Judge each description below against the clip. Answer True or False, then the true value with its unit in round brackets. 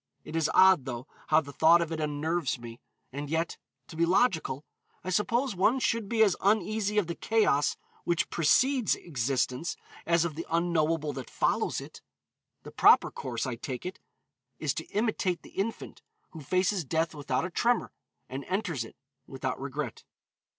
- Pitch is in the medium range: True (165 Hz)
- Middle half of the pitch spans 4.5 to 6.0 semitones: True (5.1 semitones)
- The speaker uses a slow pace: False (170 wpm)